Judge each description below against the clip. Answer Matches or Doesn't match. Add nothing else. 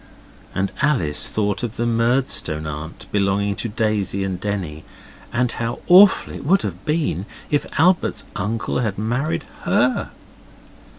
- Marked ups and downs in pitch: Doesn't match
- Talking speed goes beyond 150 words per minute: Doesn't match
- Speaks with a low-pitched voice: Matches